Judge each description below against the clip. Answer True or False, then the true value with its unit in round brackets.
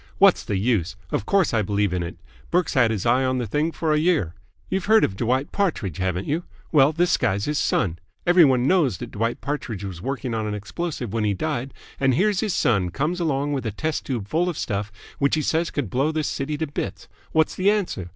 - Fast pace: True (230 wpm)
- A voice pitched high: False (135 Hz)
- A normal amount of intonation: False (7.5 semitones)